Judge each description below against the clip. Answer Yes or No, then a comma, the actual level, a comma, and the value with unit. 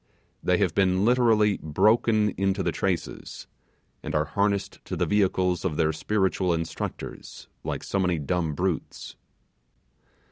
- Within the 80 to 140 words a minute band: Yes, slow, 135 wpm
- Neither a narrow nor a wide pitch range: Yes, average, 3.4 semitones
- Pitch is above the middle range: No, very low, 95 Hz